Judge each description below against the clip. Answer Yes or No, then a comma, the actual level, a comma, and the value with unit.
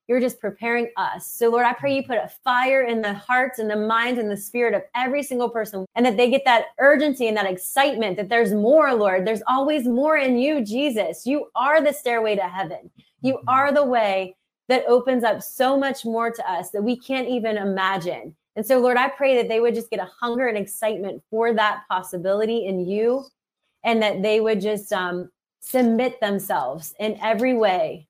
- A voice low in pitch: No, high, 230 Hz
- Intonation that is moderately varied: Yes, average, 3.6 semitones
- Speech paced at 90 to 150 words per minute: No, fast, 205 wpm